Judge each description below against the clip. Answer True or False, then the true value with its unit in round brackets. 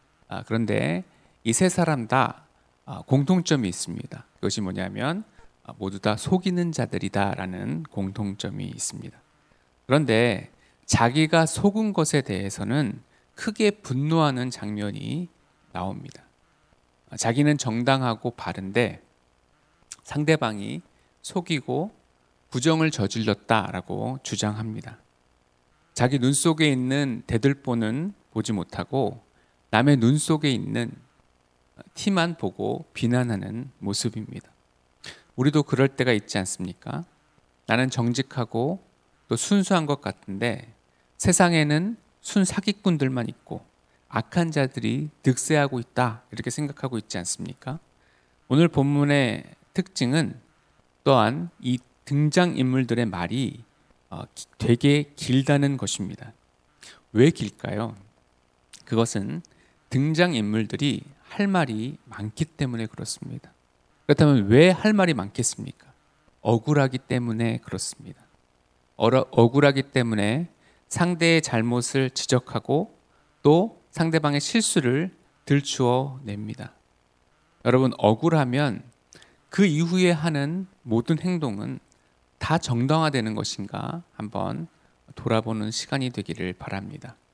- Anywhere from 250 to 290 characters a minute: False (240 characters per minute)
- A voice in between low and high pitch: False (125 Hz)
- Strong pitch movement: True (6.5 semitones)